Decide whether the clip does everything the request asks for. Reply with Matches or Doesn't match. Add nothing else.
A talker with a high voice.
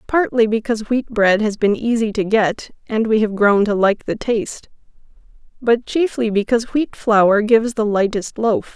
Matches